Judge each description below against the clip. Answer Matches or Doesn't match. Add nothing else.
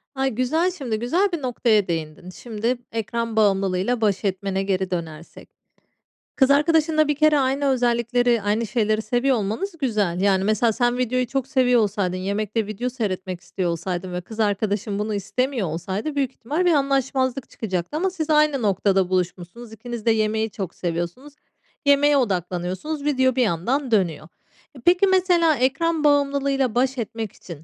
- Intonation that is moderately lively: Doesn't match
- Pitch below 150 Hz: Doesn't match